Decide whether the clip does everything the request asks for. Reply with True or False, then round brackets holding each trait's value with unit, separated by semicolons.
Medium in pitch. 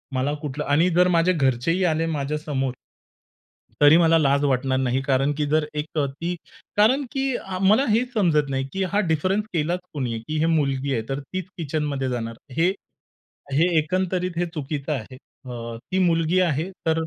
True (155 Hz)